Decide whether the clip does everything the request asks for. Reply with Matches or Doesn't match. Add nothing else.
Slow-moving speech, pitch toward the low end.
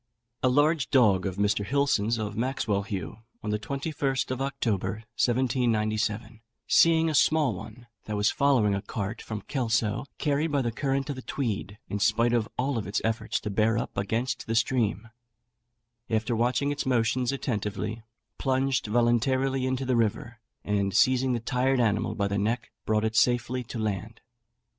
Doesn't match